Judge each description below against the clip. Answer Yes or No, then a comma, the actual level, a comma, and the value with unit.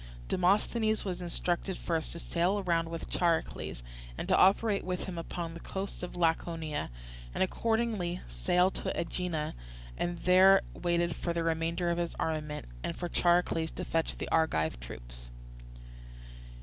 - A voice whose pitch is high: No, medium, 170 Hz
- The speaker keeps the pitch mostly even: Yes, narrow, 2.0 semitones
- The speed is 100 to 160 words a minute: Yes, average, 150 wpm